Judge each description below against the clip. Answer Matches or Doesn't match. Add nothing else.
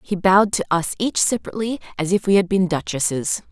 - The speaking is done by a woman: Matches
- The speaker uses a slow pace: Doesn't match